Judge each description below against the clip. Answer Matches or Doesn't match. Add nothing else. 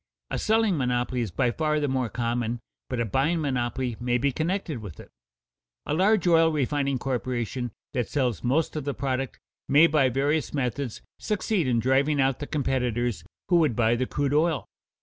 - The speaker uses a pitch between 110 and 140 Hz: Matches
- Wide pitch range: Doesn't match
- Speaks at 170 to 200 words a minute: Matches